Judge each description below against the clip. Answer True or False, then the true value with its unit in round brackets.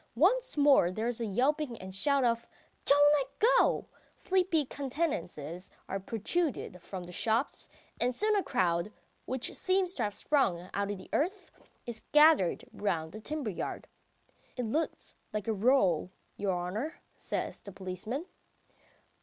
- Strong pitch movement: True (7.6 semitones)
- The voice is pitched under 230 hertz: False (235 Hz)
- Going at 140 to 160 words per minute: True (155 wpm)